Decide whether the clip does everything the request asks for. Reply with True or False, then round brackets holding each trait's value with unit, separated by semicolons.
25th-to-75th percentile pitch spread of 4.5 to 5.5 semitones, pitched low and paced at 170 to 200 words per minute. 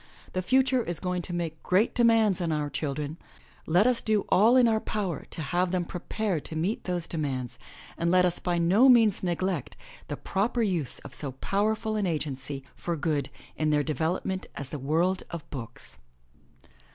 False (5.1 semitones; 175 Hz; 180 wpm)